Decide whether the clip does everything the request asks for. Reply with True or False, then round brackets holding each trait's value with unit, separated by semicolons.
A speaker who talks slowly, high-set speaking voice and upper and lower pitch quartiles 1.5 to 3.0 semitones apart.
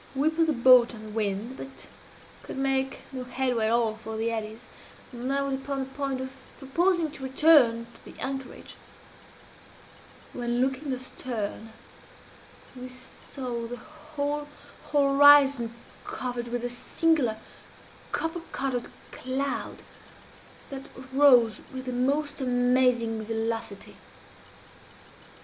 True (125 wpm; 255 Hz; 2.7 semitones)